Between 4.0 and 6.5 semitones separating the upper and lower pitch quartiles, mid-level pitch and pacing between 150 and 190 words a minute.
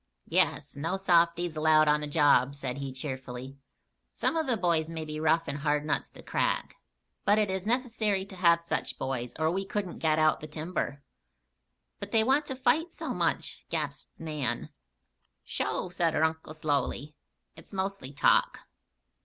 Yes: average, 4.5 semitones; medium, 160 Hz; average, 170 wpm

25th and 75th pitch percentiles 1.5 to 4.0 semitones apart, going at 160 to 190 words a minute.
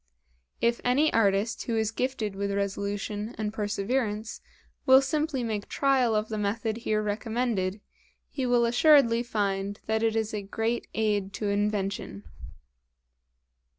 No: narrow, 2.6 semitones; slow, 135 wpm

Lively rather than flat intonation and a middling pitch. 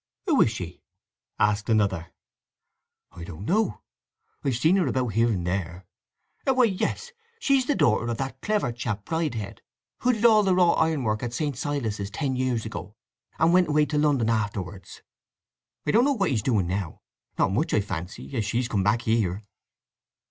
No: wide, 8.0 semitones; low, 120 Hz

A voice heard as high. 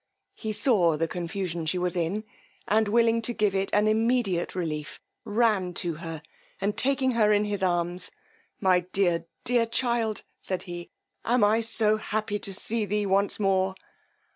Yes: high, 200 Hz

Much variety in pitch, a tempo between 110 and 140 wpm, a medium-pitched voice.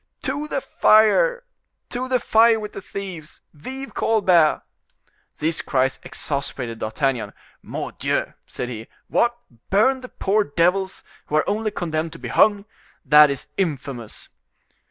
Yes: wide, 7.3 semitones; slow, 135 wpm; medium, 180 Hz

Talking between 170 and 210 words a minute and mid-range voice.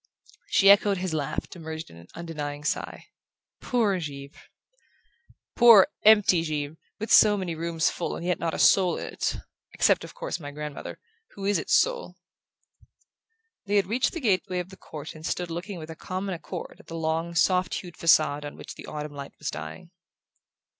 Yes: average, 190 wpm; medium, 170 Hz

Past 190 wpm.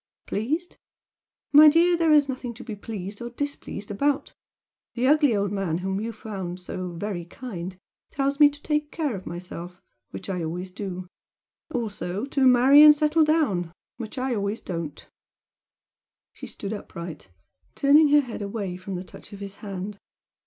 No: average, 165 wpm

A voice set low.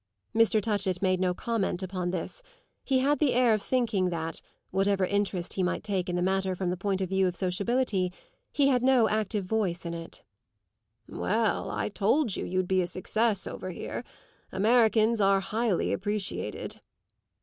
No: high, 195 Hz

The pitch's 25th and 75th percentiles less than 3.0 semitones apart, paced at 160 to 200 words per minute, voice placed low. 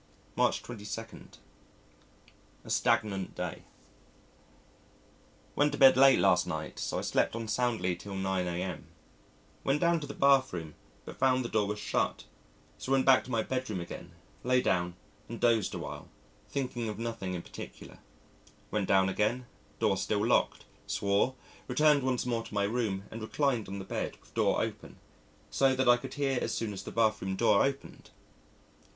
No: average, 4.8 semitones; average, 170 wpm; low, 115 Hz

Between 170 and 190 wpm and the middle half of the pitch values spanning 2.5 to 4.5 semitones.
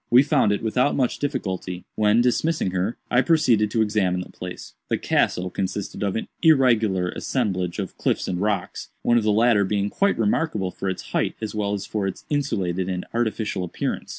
Yes: average, 185 wpm; average, 4.2 semitones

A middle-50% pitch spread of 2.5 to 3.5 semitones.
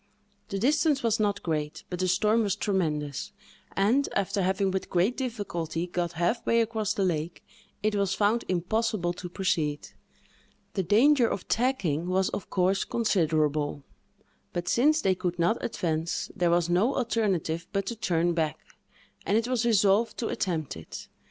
No: average, 4.4 semitones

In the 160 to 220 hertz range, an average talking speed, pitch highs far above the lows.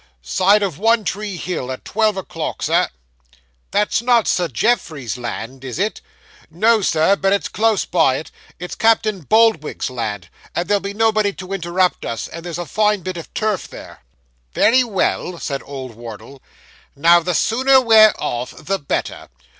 Yes: medium, 185 Hz; average, 165 wpm; wide, 6.9 semitones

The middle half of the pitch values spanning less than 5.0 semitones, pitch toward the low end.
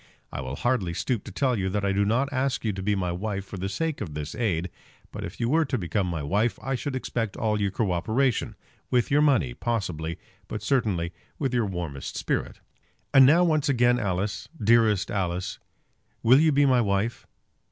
No: wide, 5.5 semitones; low, 110 Hz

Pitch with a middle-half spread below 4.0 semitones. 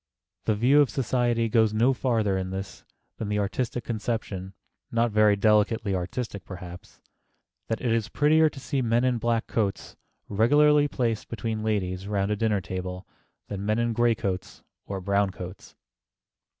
Yes: average, 3.1 semitones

